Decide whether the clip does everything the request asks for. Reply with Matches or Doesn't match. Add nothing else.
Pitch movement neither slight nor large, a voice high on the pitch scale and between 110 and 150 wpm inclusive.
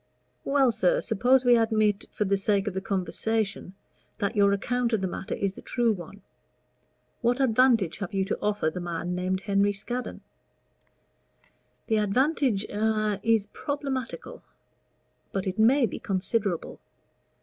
Matches